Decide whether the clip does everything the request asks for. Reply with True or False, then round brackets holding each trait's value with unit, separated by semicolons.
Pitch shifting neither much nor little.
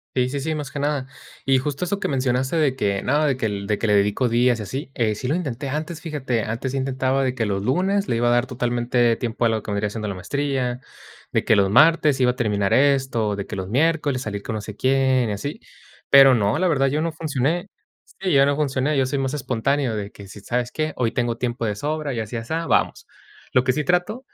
True (4.1 semitones)